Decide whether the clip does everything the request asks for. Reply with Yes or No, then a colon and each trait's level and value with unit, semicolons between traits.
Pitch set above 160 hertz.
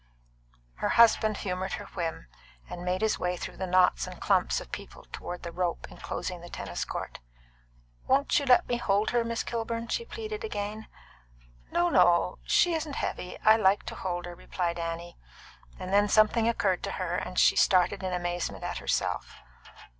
Yes: high, 190 Hz